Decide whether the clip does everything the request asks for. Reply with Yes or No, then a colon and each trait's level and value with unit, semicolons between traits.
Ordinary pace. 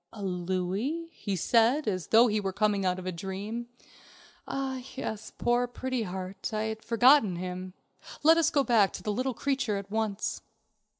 Yes: average, 175 wpm